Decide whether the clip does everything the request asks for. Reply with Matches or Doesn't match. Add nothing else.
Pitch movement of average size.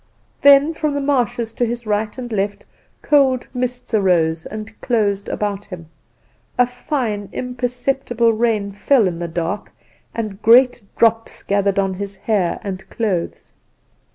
Matches